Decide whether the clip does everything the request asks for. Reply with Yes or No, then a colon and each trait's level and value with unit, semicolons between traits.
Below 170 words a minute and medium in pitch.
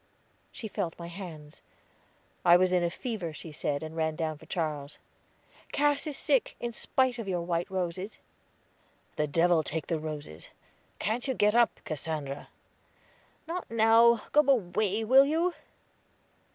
Yes: average, 150 wpm; medium, 180 Hz